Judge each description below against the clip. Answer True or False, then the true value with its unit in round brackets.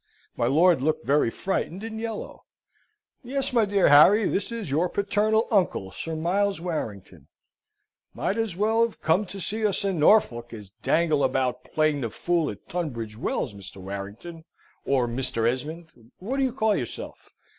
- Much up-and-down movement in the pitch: True (8.2 semitones)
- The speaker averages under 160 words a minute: False (165 wpm)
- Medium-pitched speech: True (165 Hz)